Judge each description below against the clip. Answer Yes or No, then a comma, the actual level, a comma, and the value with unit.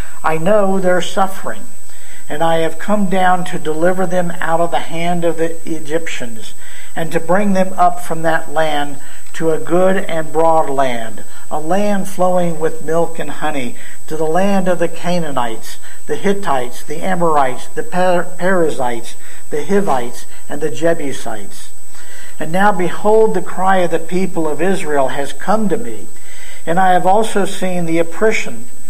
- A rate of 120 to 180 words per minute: Yes, average, 165 wpm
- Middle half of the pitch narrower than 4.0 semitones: Yes, average, 3.1 semitones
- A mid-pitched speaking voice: Yes, medium, 170 Hz